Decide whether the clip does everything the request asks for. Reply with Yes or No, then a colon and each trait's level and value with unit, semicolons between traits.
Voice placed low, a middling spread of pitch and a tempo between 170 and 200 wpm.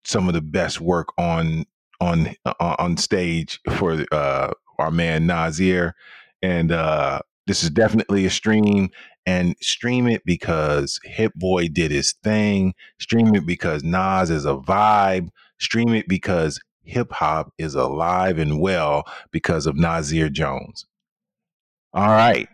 No: very low, 90 Hz; average, 3.3 semitones; average, 140 wpm